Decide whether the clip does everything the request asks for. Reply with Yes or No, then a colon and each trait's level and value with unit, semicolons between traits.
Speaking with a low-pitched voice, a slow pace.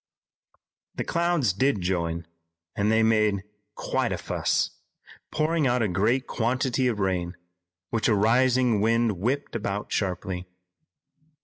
Yes: low, 110 Hz; slow, 125 wpm